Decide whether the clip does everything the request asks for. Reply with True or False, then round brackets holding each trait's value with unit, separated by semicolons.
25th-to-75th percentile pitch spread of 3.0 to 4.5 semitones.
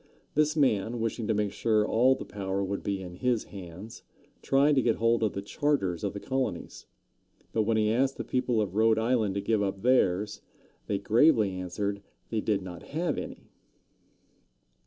True (3.6 semitones)